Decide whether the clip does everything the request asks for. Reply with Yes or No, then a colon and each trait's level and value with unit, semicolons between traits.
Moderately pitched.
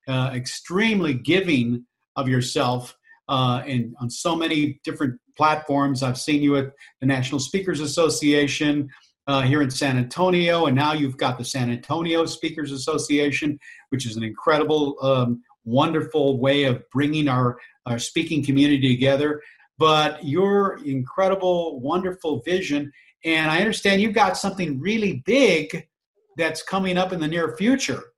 Yes: medium, 150 Hz